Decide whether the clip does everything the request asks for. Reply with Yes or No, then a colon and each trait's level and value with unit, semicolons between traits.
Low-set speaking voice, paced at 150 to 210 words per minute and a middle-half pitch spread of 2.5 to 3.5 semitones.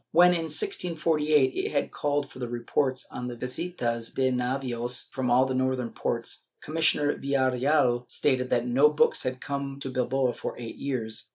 Yes: low, 130 Hz; average, 165 wpm; average, 2.9 semitones